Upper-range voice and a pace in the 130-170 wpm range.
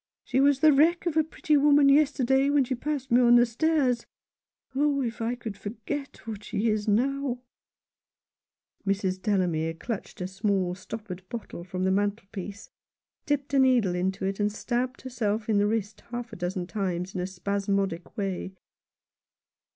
Yes: high, 220 Hz; average, 165 wpm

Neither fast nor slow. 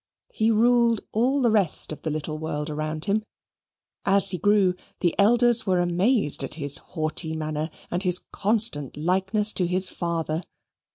Yes: average, 165 wpm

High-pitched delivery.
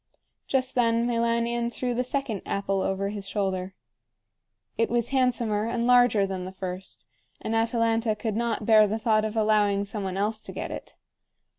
Yes: high, 220 Hz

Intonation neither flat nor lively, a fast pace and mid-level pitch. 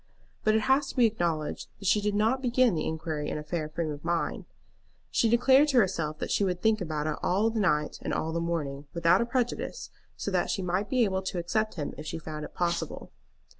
No: wide, 5.8 semitones; fast, 235 wpm; medium, 180 Hz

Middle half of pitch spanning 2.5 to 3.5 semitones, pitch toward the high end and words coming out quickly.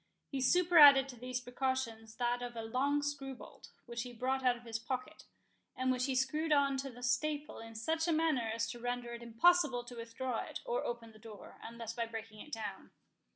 Yes: average, 3.1 semitones; very high, 250 Hz; fast, 210 wpm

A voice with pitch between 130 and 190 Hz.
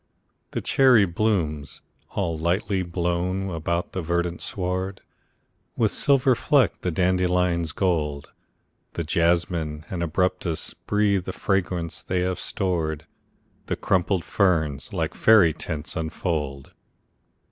No: very low, 90 Hz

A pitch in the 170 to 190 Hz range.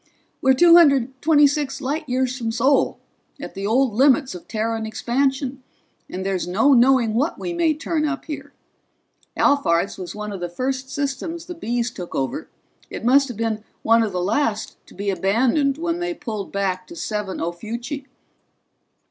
No: very high, 250 Hz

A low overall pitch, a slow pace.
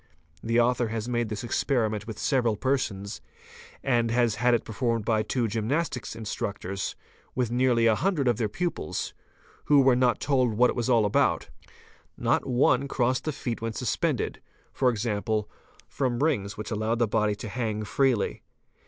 No: low, 120 Hz; average, 160 wpm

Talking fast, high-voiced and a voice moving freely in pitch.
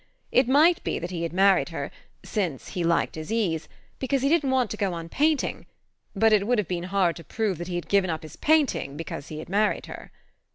Yes: fast, 235 wpm; high, 195 Hz; wide, 6.5 semitones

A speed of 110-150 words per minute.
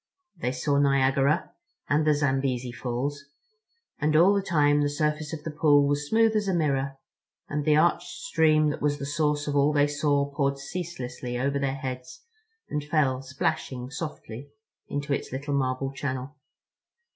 No: average, 165 wpm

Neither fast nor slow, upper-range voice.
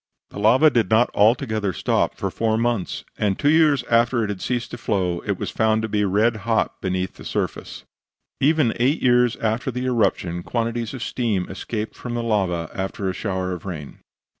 No: average, 190 wpm; low, 110 Hz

